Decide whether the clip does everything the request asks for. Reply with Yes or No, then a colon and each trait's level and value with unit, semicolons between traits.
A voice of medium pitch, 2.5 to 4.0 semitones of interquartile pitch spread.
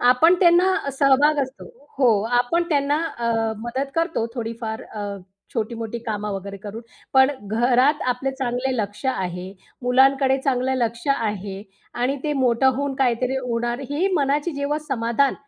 No: very high, 255 Hz; average, 3.3 semitones